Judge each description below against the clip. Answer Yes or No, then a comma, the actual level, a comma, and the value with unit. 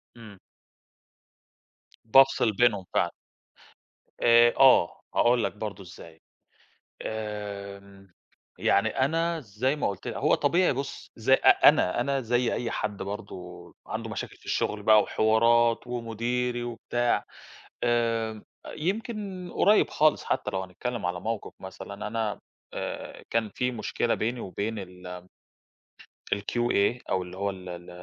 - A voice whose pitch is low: Yes, low, 115 Hz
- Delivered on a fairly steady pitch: No, average, 3.6 semitones